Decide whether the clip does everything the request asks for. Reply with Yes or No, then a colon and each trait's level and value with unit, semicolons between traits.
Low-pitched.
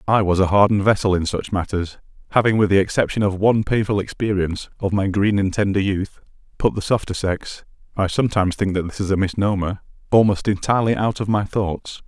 Yes: low, 100 Hz